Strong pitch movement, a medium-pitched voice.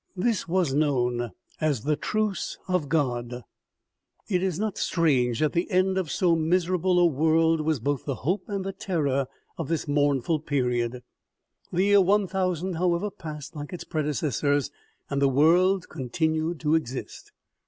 No: average, 4.4 semitones; medium, 160 Hz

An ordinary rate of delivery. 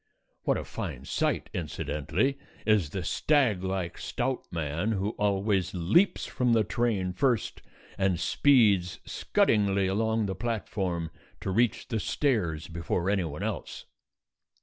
No: slow, 130 wpm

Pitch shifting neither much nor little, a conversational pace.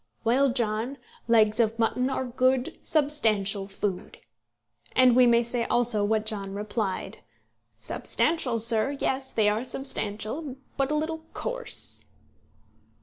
No: average, 3.8 semitones; slow, 125 wpm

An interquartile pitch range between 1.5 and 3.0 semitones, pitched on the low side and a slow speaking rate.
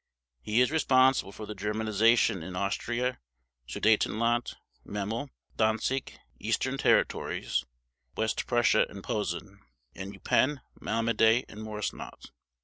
Yes: narrow, 2.6 semitones; low, 110 Hz; slow, 100 wpm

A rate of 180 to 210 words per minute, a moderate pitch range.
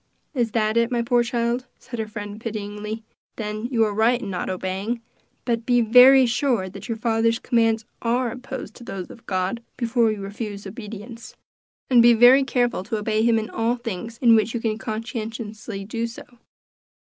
No: average, 185 wpm; narrow, 1.9 semitones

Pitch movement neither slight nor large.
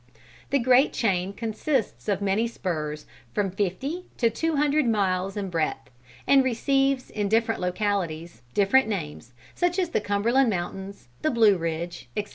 No: wide, 6.0 semitones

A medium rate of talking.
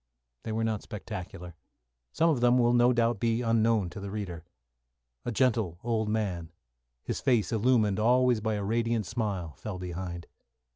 Yes: average, 160 wpm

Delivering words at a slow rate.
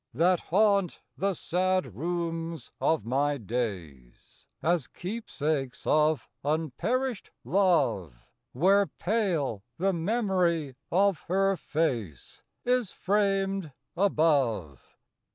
Yes: slow, 90 wpm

